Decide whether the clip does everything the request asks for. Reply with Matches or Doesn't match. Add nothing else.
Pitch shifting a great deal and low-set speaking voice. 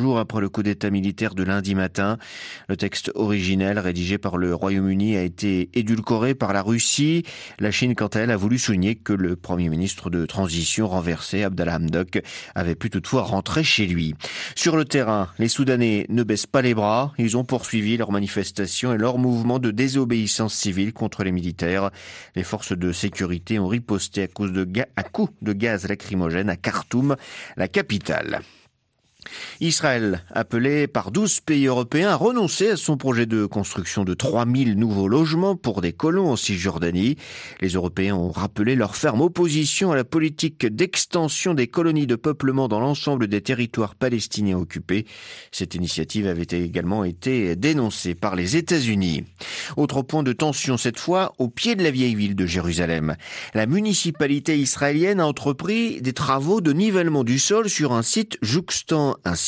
Matches